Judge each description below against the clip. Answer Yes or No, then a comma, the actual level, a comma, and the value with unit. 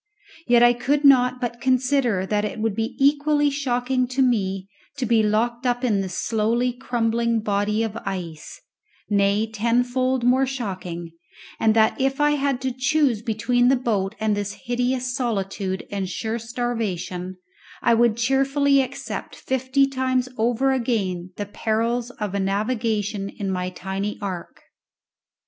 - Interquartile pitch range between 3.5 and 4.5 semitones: Yes, average, 3.8 semitones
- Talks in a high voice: Yes, high, 235 Hz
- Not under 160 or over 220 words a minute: No, average, 150 wpm